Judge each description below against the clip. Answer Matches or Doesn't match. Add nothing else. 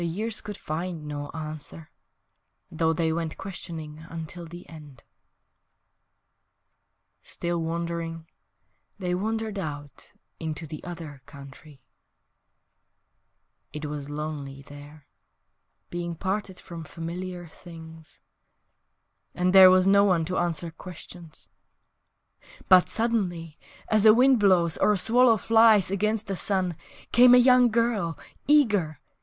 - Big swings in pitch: Doesn't match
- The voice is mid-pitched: Matches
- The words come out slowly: Matches